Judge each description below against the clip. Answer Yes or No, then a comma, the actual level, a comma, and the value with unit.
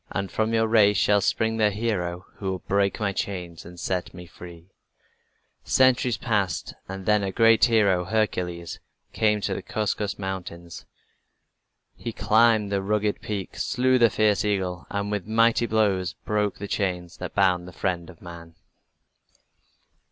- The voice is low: Yes, low, 100 Hz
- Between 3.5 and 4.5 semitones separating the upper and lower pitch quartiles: No, average, 3.1 semitones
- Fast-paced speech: No, average, 155 wpm